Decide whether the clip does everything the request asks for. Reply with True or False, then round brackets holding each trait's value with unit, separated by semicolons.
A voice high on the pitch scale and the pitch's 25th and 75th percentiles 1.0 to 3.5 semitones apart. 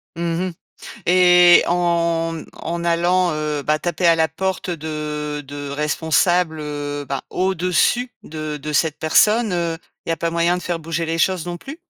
False (165 Hz; 2.5 semitones)